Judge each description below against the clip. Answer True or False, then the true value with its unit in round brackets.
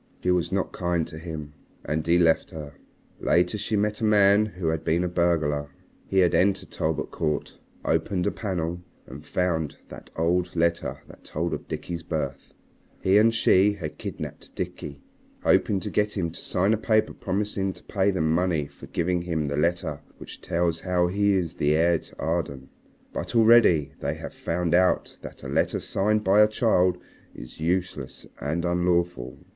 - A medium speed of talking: True (175 wpm)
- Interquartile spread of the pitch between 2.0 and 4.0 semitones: True (3.1 semitones)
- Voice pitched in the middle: False (90 Hz)